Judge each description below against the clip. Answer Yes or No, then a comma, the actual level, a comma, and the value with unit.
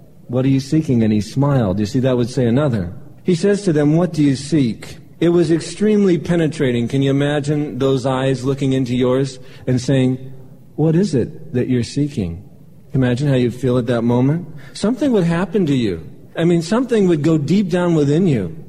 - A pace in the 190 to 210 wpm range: Yes, average, 200 wpm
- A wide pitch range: No, average, 4.3 semitones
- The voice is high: No, medium, 140 Hz